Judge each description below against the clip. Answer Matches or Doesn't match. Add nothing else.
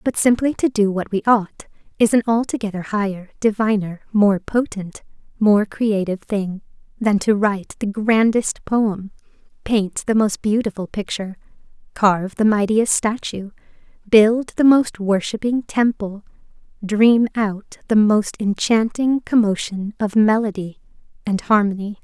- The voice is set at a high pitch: Matches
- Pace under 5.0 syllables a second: Matches